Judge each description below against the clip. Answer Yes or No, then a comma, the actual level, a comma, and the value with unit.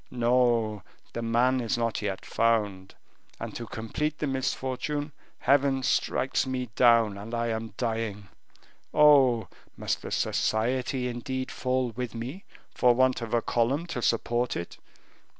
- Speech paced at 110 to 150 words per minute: Yes, average, 140 wpm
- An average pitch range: No, narrow, 2.3 semitones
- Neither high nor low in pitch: No, low, 120 Hz